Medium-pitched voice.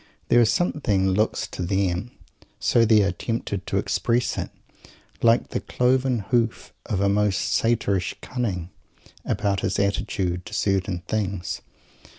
No: low, 100 Hz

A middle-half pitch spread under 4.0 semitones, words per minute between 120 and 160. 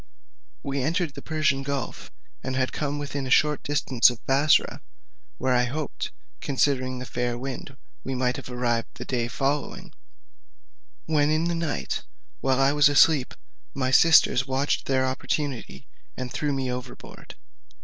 Yes: narrow, 2.4 semitones; average, 150 wpm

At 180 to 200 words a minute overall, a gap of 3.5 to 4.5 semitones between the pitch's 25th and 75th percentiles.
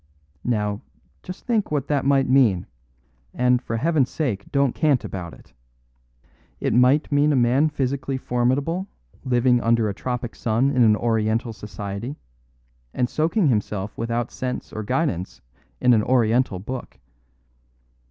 No: average, 140 wpm; average, 3.9 semitones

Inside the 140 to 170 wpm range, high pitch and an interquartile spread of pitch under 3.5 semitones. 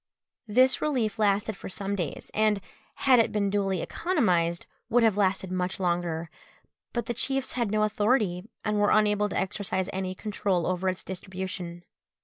Yes: average, 165 wpm; high, 200 Hz; average, 2.7 semitones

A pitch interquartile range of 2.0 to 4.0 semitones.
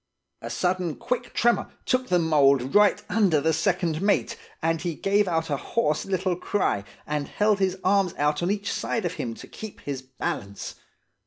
No: average, 5.1 semitones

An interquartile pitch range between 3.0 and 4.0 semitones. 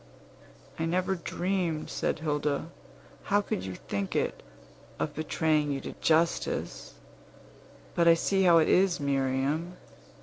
Yes: average, 3.5 semitones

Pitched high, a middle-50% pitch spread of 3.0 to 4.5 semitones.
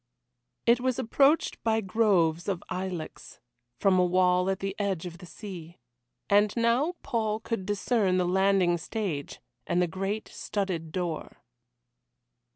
Yes: high, 195 Hz; average, 3.4 semitones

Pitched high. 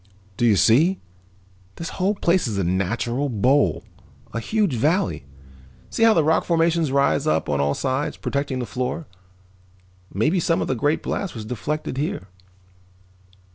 No: medium, 140 Hz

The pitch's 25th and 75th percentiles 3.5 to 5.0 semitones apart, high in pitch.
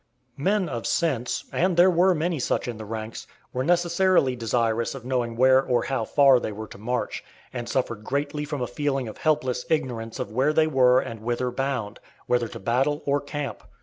No: average, 3.9 semitones; low, 130 Hz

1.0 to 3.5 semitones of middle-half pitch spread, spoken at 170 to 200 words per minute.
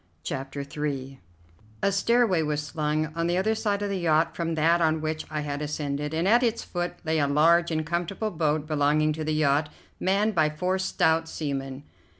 Yes: average, 2.7 semitones; average, 190 wpm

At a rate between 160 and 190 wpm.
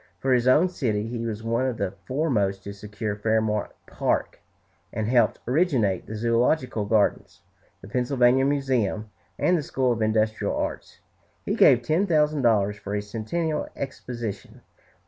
No: average, 150 wpm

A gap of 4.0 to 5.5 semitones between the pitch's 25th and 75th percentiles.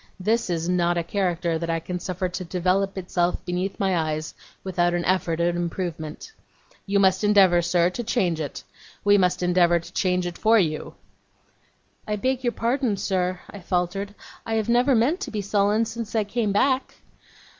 No: average, 3.2 semitones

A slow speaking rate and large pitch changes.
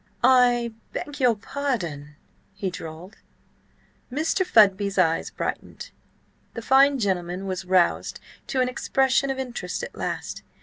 Yes: slow, 125 wpm; wide, 6.3 semitones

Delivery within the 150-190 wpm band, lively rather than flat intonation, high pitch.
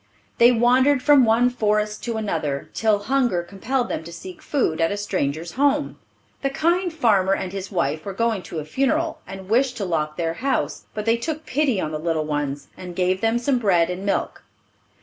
No: average, 200 wpm; wide, 6.5 semitones; high, 210 Hz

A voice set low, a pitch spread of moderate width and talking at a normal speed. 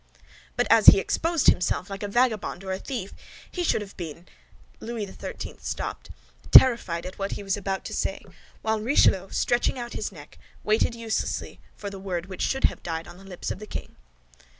No: high, 200 Hz; average, 3.6 semitones; average, 190 wpm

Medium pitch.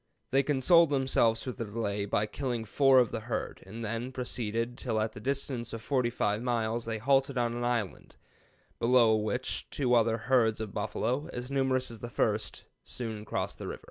No: low, 120 Hz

